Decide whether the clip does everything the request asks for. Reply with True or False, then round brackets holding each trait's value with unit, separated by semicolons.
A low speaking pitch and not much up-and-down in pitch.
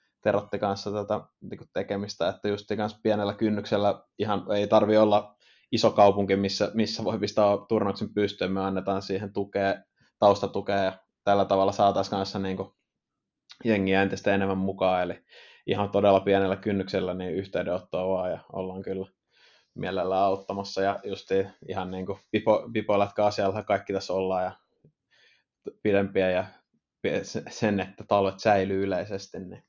True (100 Hz; 1.2 semitones)